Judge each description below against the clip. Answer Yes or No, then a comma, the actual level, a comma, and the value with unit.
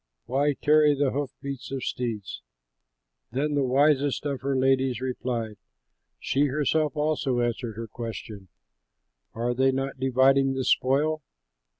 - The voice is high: No, low, 135 Hz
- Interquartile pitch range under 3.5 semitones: Yes, narrow, 2.5 semitones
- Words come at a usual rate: No, slow, 130 wpm